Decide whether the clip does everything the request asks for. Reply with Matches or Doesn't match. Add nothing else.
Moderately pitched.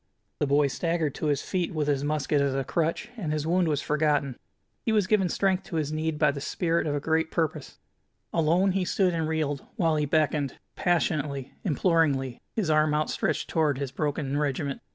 Matches